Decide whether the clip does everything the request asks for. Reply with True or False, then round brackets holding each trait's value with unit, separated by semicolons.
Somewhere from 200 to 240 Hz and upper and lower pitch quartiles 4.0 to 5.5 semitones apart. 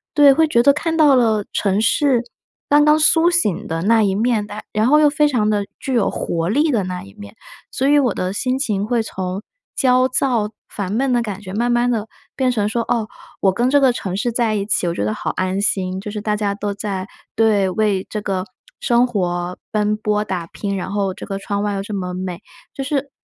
True (210 Hz; 4.3 semitones)